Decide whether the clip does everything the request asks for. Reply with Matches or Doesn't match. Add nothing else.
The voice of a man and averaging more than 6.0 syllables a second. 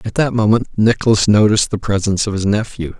Matches